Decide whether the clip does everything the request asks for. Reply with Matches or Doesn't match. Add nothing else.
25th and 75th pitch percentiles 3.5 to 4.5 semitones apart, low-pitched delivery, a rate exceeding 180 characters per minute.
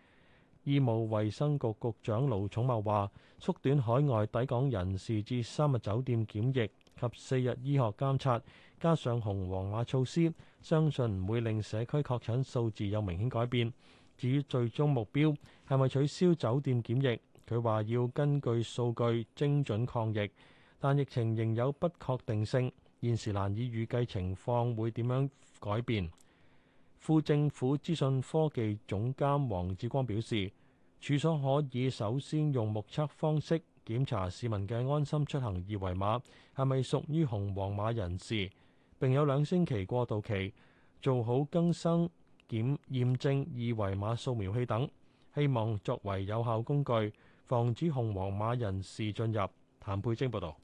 Matches